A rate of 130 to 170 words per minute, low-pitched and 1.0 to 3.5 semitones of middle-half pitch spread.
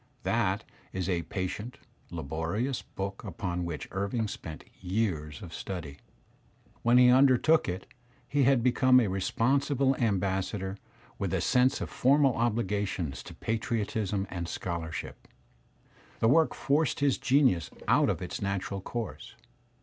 No: average, 140 wpm; low, 100 Hz; wide, 5.6 semitones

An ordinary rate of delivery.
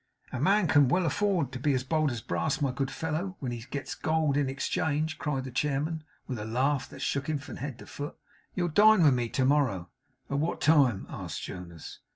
No: fast, 215 wpm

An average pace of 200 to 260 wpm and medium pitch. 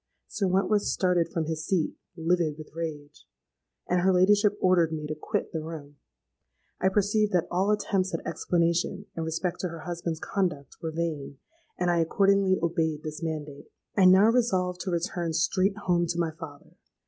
No: average, 170 wpm; medium, 170 Hz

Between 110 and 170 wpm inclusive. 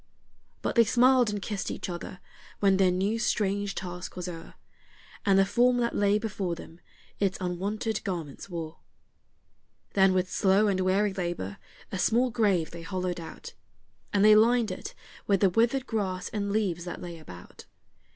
Yes: average, 165 wpm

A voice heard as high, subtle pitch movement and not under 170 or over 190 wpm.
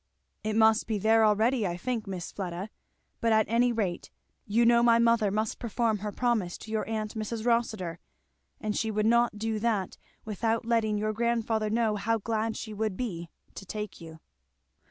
Yes: high, 220 Hz; narrow, 1.7 semitones; average, 180 wpm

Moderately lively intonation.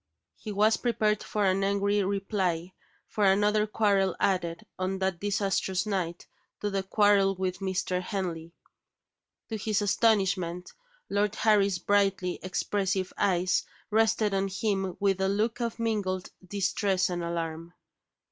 No: narrow, 1.9 semitones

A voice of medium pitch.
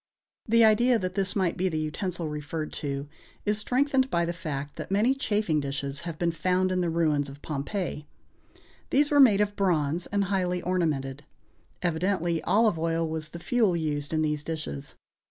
Yes: medium, 170 Hz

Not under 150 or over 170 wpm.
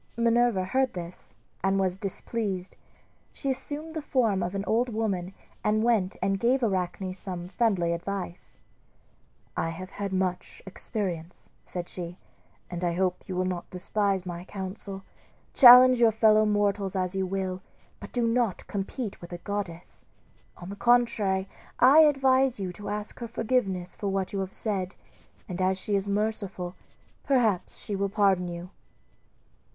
Yes: average, 155 wpm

